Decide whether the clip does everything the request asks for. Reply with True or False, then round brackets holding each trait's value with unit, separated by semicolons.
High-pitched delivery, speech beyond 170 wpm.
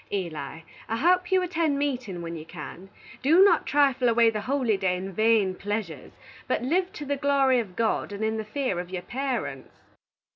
True (230 Hz; 190 wpm)